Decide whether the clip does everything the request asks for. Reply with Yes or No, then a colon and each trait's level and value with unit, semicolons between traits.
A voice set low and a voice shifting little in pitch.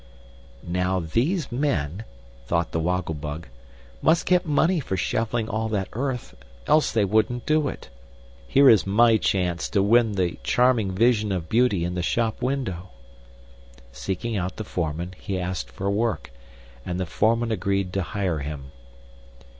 No: low, 100 Hz; average, 5.0 semitones